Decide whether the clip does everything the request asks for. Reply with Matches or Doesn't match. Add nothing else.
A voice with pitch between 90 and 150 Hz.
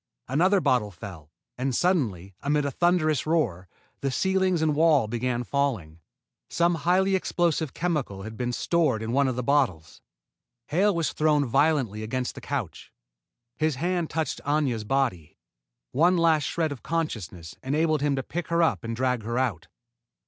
Matches